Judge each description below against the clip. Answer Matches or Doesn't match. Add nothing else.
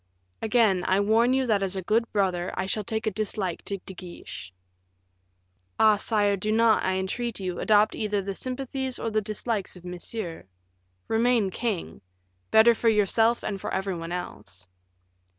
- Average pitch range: Matches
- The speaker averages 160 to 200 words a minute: Matches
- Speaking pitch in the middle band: Doesn't match